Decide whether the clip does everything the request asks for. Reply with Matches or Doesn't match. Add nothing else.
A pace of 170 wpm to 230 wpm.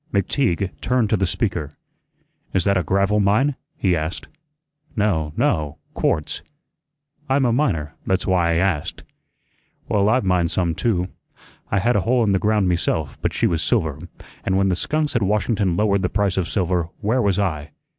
Matches